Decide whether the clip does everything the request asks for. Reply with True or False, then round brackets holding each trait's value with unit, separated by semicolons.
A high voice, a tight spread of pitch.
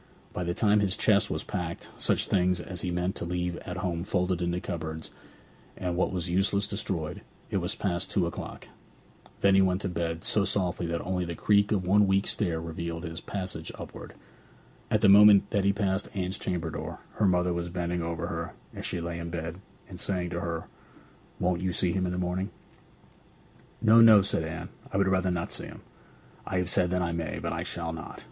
False (90 Hz; 2.1 semitones)